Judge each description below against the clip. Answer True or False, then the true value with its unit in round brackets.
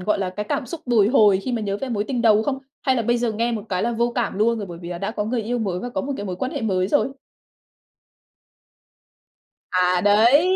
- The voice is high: True (220 Hz)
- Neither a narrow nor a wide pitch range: True (3.4 semitones)